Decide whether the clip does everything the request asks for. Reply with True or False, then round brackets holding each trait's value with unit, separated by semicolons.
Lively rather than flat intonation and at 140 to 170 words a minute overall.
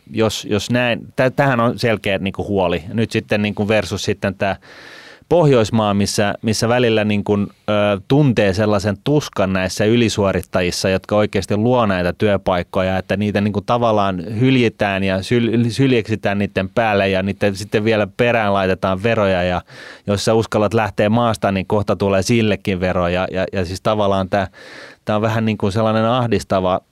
False (2.6 semitones; 155 wpm)